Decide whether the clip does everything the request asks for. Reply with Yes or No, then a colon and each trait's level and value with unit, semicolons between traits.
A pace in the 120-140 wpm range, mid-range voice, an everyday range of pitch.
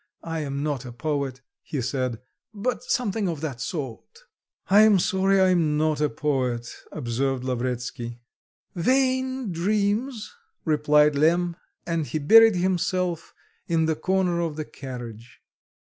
No: slow, 135 wpm; medium, 155 Hz; wide, 5.9 semitones